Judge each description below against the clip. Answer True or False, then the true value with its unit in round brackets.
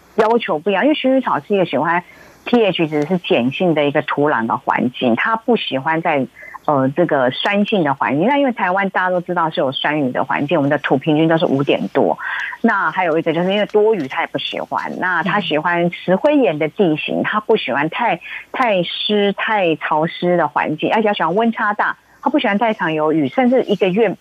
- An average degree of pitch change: False (6.0 semitones)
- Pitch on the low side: False (185 Hz)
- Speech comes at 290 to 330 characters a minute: True (320 characters per minute)